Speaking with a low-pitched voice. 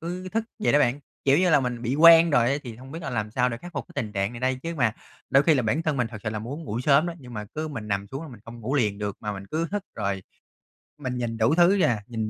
Yes: low, 125 Hz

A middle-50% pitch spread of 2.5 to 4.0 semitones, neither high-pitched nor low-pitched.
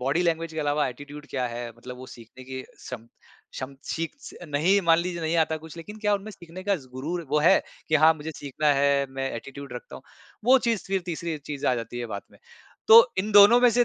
No: average, 4.9 semitones; medium, 155 Hz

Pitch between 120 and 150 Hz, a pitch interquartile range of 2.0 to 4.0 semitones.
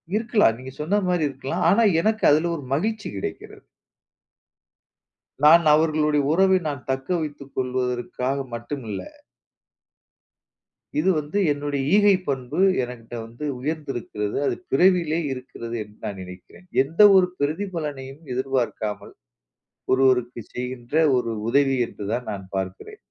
No: low, 135 Hz; average, 4.6 semitones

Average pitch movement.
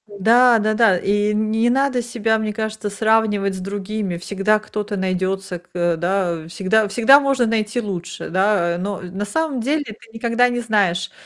Yes: average, 3.0 semitones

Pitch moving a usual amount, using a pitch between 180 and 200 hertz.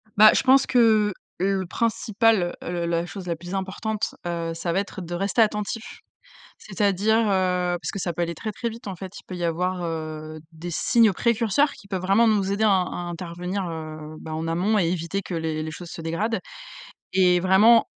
Yes: average, 3.7 semitones; medium, 185 Hz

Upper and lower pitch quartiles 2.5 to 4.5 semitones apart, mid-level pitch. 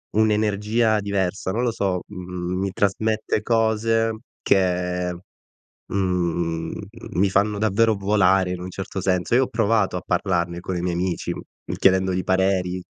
No: average, 2.9 semitones; very low, 95 Hz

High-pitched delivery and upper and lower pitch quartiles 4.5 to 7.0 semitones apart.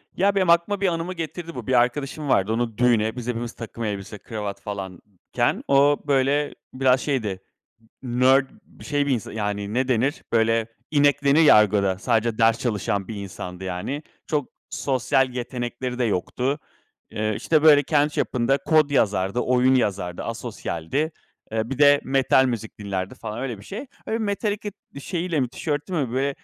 No: low, 125 Hz; average, 5.0 semitones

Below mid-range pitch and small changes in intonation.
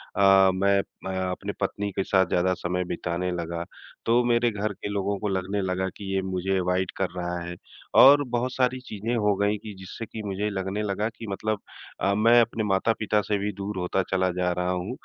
Yes: low, 100 Hz; narrow, 2.3 semitones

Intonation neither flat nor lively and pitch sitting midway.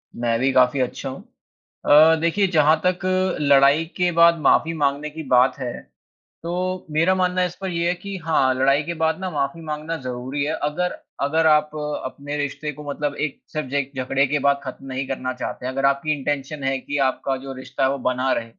Yes: average, 3.3 semitones; medium, 145 Hz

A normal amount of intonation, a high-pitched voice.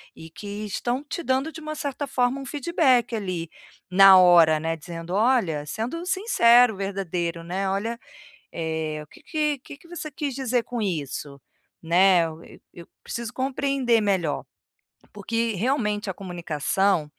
No: wide, 7.3 semitones; high, 210 Hz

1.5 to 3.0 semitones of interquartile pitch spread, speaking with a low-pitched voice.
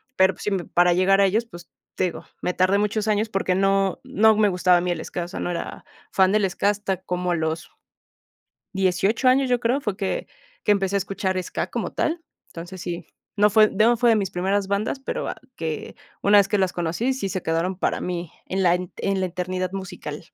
No: narrow, 2.5 semitones; high, 195 Hz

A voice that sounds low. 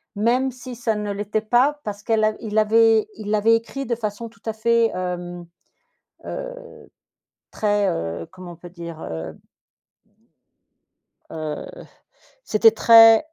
No: high, 215 Hz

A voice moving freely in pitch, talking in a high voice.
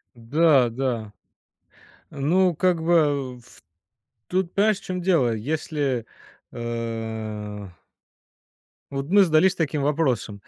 No: wide, 6.4 semitones; medium, 140 Hz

